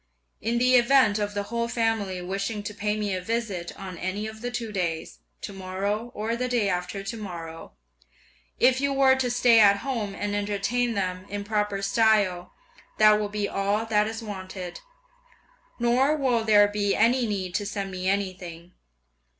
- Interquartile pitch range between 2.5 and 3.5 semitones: Yes, average, 2.9 semitones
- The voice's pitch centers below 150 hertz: No, high, 210 Hz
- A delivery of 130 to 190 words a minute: Yes, average, 175 wpm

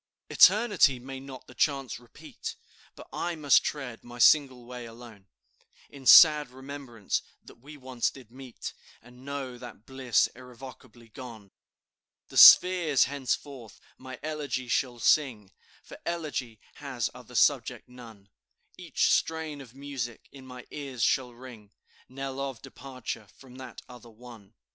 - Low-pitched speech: Yes, low, 130 Hz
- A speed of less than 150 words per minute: Yes, average, 140 wpm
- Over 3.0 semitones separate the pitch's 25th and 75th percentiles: No, narrow, 2.6 semitones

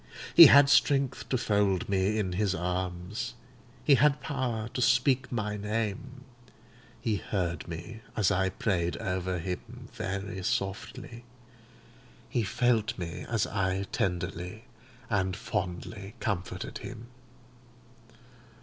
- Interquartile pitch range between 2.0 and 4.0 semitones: No, average, 4.4 semitones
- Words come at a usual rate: No, slow, 115 wpm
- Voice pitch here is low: Yes, low, 105 Hz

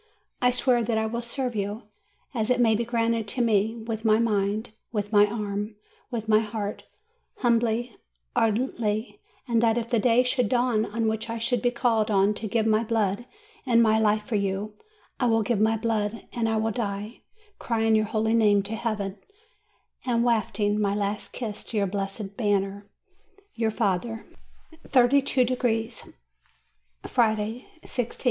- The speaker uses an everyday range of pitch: No, narrow, 2.1 semitones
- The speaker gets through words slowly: No, average, 165 wpm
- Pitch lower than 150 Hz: No, high, 220 Hz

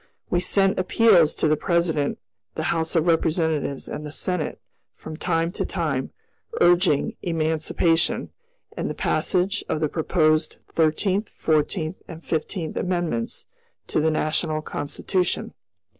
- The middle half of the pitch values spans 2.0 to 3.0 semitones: Yes, narrow, 2.4 semitones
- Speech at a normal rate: No, slow, 130 wpm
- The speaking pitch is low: No, medium, 165 Hz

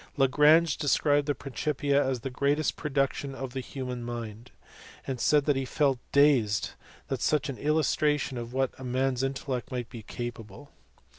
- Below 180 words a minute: Yes, average, 155 wpm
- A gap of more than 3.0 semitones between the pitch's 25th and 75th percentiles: No, average, 2.7 semitones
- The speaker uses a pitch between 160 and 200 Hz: No, low, 135 Hz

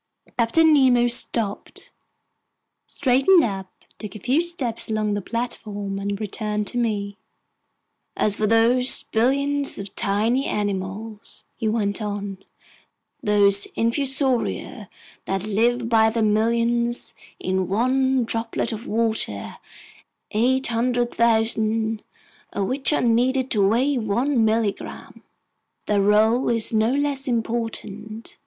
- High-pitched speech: Yes, high, 225 Hz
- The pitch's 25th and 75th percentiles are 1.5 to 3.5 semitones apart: Yes, average, 2.8 semitones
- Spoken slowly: Yes, slow, 110 wpm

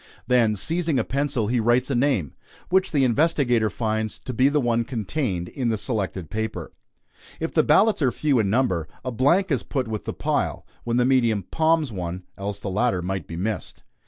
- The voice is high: No, low, 120 Hz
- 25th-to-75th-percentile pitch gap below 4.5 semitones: No, average, 5.0 semitones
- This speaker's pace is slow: No, average, 195 wpm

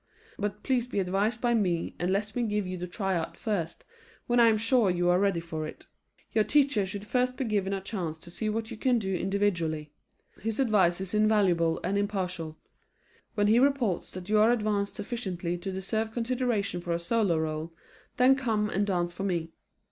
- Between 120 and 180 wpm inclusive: No, average, 195 wpm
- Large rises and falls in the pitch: No, average, 4.0 semitones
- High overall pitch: Yes, high, 200 Hz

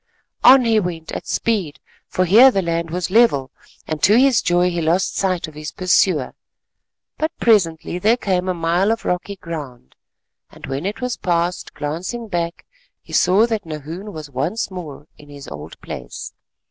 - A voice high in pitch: No, medium, 180 Hz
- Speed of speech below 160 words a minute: No, average, 170 wpm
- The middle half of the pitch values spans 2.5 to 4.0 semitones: No, average, 4.7 semitones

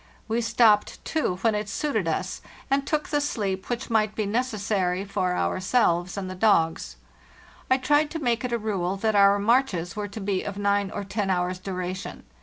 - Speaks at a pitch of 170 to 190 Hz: No, high, 205 Hz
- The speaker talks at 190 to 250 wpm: Yes, average, 195 wpm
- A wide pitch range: No, average, 3.8 semitones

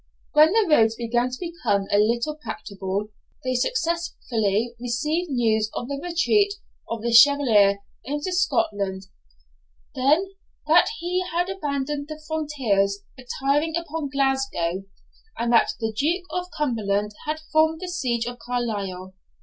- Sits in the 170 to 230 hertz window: No, very high, 260 Hz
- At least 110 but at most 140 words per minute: Yes, slow, 135 wpm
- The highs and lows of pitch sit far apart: Yes, wide, 6.3 semitones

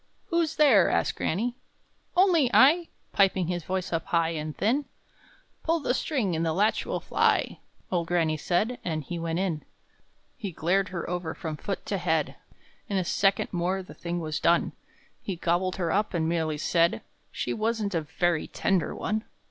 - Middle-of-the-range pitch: Yes, medium, 180 Hz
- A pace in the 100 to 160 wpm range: No, average, 175 wpm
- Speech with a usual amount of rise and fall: Yes, average, 4.1 semitones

